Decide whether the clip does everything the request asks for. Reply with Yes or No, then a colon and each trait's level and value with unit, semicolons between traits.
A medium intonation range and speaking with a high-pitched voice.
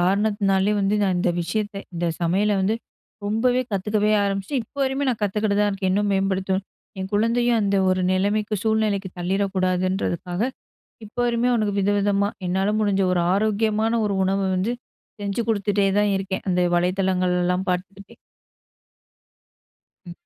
No: narrow, 2.0 semitones; high, 200 Hz